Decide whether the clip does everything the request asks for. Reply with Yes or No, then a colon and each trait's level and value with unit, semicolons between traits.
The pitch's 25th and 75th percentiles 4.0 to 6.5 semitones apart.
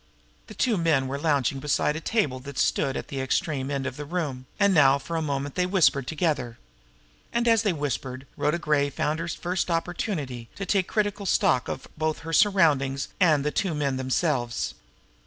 Yes: average, 4.4 semitones